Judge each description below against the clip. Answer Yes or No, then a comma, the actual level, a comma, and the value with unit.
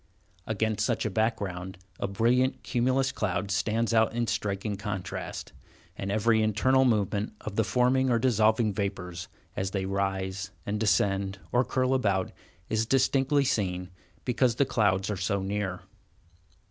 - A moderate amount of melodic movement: Yes, average, 3.3 semitones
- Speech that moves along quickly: No, average, 145 wpm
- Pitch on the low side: Yes, low, 105 Hz